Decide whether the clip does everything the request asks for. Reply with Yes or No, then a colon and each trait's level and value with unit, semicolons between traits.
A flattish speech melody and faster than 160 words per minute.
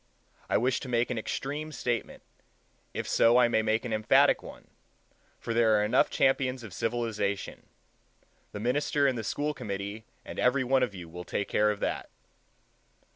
No: average, 3.2 semitones; average, 175 wpm